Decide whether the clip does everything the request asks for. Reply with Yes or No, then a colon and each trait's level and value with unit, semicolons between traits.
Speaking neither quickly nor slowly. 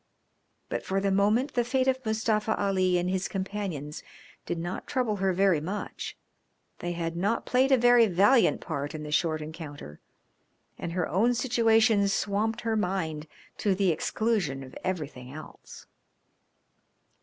Yes: average, 150 wpm